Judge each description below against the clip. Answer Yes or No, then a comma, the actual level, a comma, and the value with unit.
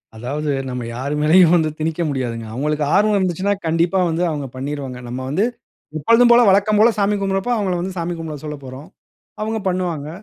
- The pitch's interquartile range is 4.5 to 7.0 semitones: Yes, average, 5.2 semitones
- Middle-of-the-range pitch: Yes, medium, 165 Hz